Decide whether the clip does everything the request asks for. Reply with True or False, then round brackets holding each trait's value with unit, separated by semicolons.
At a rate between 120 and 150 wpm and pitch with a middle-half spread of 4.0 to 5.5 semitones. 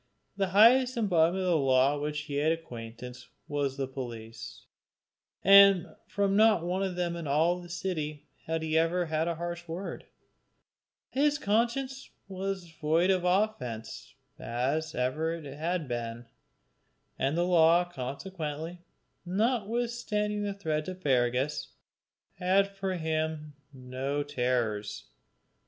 True (135 wpm; 5.1 semitones)